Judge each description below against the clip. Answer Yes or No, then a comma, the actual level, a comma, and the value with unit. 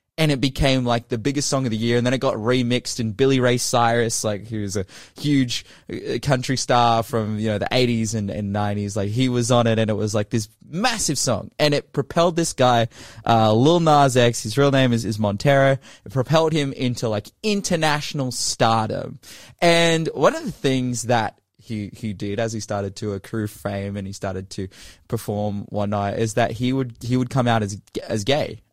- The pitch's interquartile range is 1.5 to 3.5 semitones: No, average, 3.9 semitones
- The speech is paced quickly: Yes, fast, 210 wpm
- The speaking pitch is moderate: No, low, 120 Hz